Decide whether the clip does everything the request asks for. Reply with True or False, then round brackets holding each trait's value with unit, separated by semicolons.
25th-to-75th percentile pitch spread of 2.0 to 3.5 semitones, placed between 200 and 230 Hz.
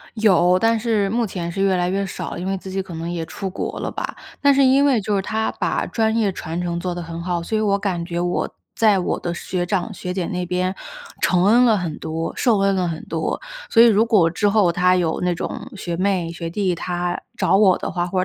False (3.0 semitones; 185 Hz)